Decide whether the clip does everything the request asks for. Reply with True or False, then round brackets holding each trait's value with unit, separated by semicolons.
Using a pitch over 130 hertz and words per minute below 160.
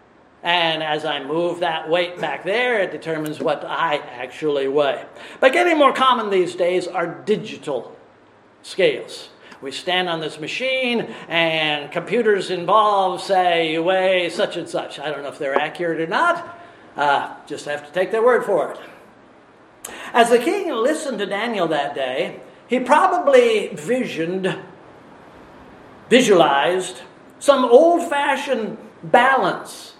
True (185 Hz; 140 wpm)